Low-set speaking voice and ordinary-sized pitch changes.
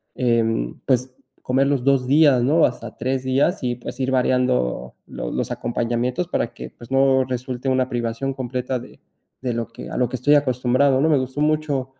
No: low, 130 Hz; narrow, 1.8 semitones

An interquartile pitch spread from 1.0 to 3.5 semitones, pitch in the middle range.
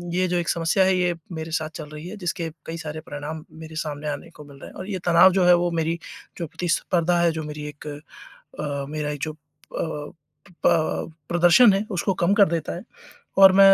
Yes: average, 2.8 semitones; medium, 165 Hz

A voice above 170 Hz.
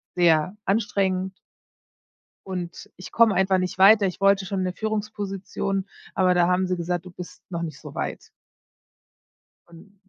Yes: medium, 185 Hz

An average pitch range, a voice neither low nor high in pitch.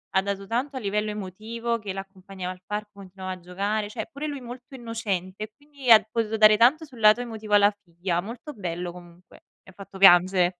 No: average, 3.6 semitones; high, 210 Hz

